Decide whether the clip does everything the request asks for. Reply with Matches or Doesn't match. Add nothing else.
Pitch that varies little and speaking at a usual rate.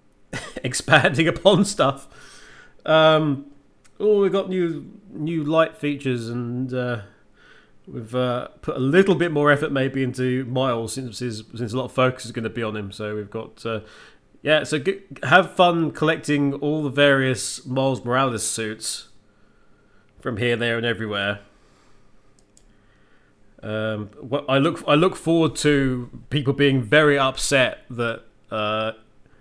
Doesn't match